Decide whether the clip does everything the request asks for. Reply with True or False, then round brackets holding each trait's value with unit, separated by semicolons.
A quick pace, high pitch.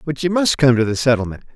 False (270 wpm; 135 Hz)